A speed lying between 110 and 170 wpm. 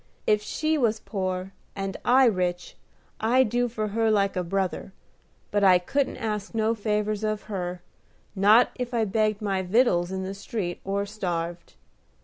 Yes: average, 160 wpm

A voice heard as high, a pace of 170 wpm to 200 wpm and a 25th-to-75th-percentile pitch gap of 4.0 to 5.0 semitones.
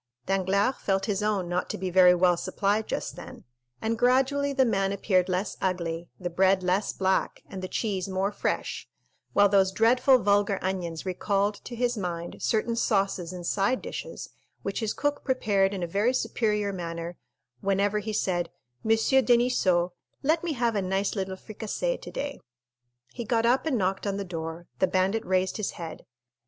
No: high, 195 Hz; average, 175 wpm; average, 3.3 semitones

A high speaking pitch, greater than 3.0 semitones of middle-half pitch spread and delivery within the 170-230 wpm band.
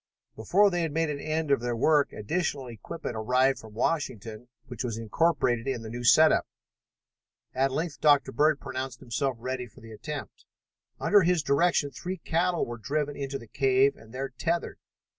No: low, 135 Hz; average, 4.6 semitones; average, 180 wpm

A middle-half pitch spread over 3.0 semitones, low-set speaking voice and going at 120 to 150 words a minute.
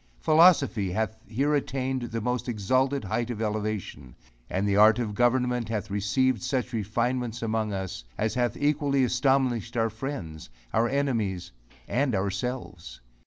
Yes: average, 3.8 semitones; low, 115 Hz; average, 140 wpm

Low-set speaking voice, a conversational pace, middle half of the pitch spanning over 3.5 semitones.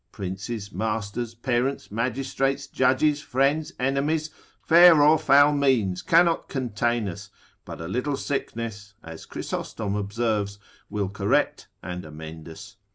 No: low, 120 Hz; slow, 120 wpm; wide, 5.6 semitones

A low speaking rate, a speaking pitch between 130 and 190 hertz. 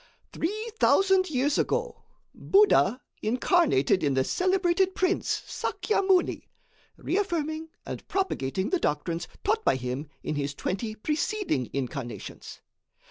No: slow, 115 wpm; very high, 310 Hz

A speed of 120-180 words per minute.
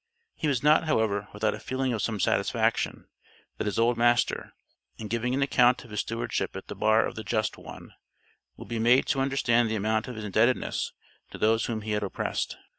No: fast, 205 wpm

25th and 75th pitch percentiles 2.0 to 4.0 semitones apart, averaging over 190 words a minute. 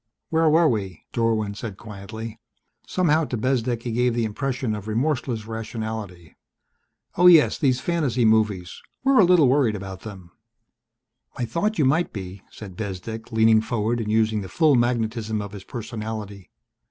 No: average, 3.4 semitones; average, 155 wpm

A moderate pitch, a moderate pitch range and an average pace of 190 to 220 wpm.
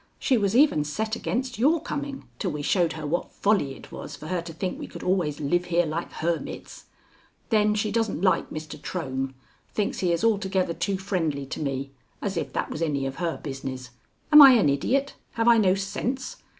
No: medium, 180 Hz; wide, 6.2 semitones; fast, 205 wpm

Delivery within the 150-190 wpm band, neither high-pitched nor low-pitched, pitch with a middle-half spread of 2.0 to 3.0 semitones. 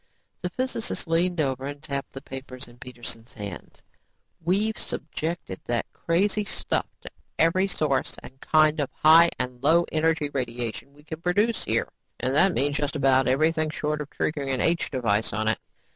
No: average, 170 wpm; medium, 150 Hz; average, 4.2 semitones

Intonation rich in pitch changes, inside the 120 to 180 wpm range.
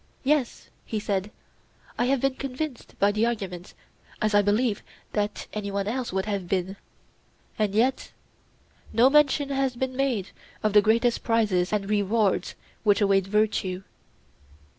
No: average, 4.0 semitones; average, 145 wpm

